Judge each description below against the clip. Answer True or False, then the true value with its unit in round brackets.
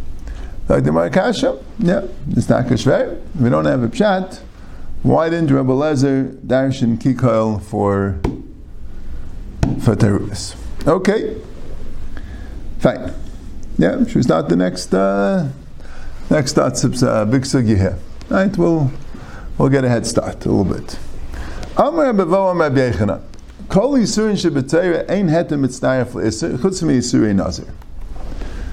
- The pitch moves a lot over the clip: True (7.3 semitones)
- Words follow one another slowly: False (150 wpm)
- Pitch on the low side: True (110 Hz)